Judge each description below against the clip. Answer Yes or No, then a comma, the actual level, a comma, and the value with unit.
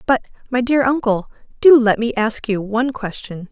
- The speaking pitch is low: No, high, 235 Hz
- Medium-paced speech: Yes, average, 190 wpm